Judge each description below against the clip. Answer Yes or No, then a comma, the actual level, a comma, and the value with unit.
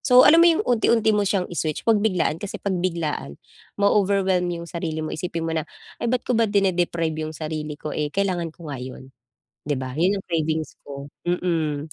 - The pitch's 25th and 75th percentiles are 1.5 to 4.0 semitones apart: No, average, 4.4 semitones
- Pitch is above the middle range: No, medium, 170 Hz